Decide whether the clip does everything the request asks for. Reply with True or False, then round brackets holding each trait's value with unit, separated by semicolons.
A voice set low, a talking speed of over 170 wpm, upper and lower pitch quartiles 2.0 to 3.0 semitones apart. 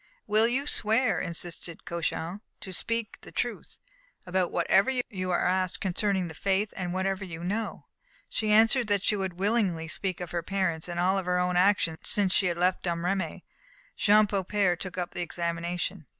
False (185 Hz; 180 wpm; 2.7 semitones)